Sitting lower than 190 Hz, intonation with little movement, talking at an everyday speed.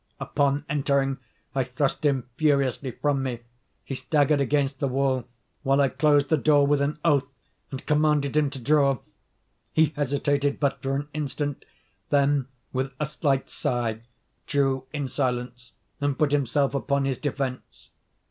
Yes: medium, 140 Hz; narrow, 1.5 semitones; average, 150 wpm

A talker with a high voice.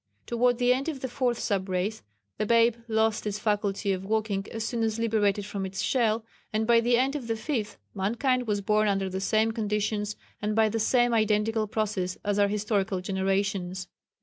Yes: high, 215 Hz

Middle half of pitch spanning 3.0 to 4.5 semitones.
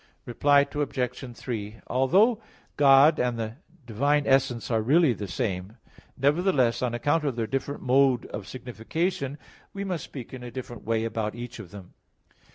Yes: average, 3.8 semitones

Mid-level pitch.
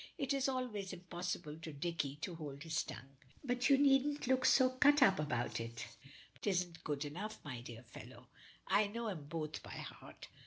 Yes: medium, 180 Hz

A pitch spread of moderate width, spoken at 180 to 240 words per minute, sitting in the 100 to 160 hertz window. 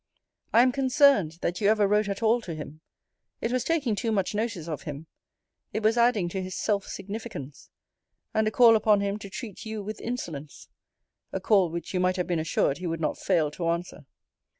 No: average, 4.6 semitones; fast, 205 wpm; high, 200 Hz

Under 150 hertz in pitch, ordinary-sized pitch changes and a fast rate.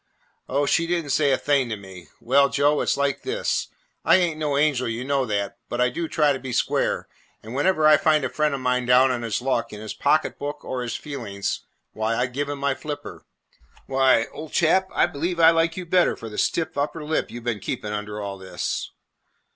Yes: medium, 140 Hz; average, 4.3 semitones; fast, 235 wpm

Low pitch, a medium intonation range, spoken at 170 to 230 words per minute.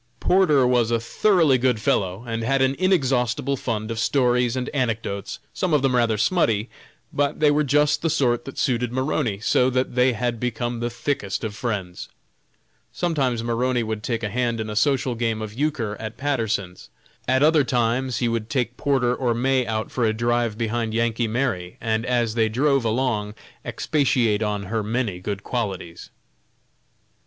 Yes: low, 120 Hz; average, 3.0 semitones; average, 175 wpm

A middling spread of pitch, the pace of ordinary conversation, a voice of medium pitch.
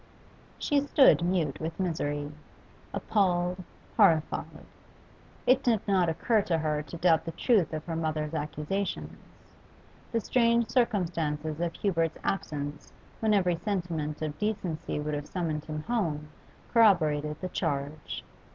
No: average, 4.6 semitones; slow, 130 wpm; medium, 165 Hz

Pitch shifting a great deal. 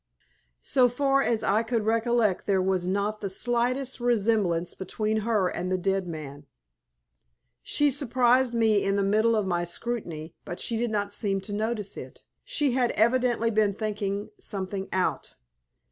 No: average, 3.6 semitones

